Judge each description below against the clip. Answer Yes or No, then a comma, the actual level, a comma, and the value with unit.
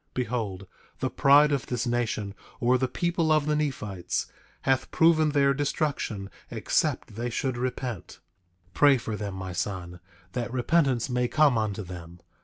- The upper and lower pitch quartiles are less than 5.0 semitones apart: No, average, 5.3 semitones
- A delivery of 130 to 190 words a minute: Yes, average, 155 wpm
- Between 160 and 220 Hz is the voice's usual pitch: No, low, 125 Hz